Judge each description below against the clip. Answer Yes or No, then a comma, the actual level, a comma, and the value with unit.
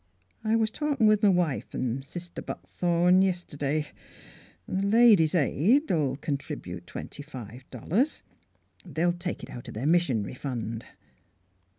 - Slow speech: Yes, slow, 130 wpm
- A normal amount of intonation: No, wide, 6.4 semitones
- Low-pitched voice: No, medium, 170 Hz